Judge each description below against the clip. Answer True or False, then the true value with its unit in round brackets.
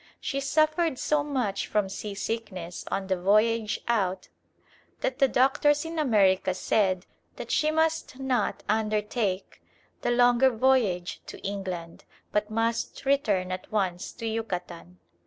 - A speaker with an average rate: False (130 wpm)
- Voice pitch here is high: True (220 Hz)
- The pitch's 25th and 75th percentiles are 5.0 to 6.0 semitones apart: True (5.6 semitones)